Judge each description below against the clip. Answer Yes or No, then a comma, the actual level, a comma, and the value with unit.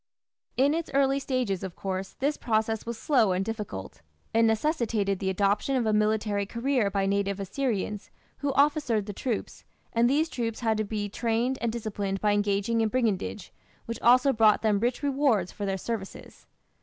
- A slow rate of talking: No, average, 175 wpm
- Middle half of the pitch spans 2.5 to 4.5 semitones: Yes, average, 3.9 semitones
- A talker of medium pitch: No, high, 220 Hz